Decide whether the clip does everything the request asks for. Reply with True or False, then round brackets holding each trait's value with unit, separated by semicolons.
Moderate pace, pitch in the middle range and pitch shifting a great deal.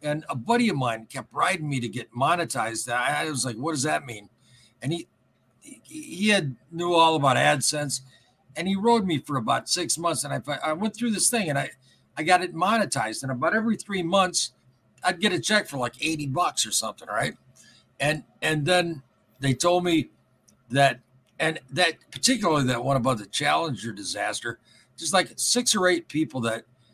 True (190 wpm; 150 Hz; 6.1 semitones)